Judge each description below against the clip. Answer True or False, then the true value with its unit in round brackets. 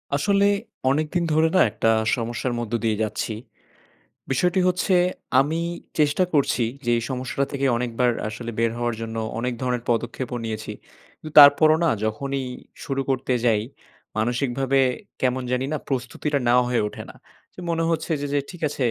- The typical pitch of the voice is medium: False (130 Hz)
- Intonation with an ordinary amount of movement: True (3.7 semitones)